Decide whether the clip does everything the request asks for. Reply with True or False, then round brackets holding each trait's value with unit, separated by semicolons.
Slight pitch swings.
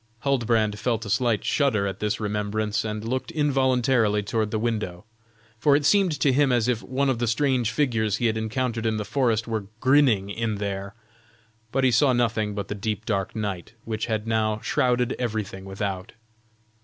False (3.1 semitones)